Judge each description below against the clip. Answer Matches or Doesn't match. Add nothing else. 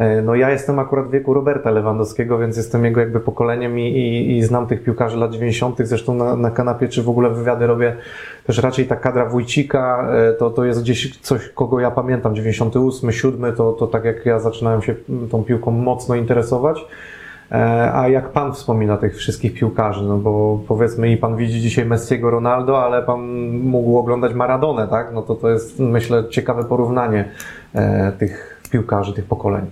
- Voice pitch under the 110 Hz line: Doesn't match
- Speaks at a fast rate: Matches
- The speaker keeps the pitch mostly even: Matches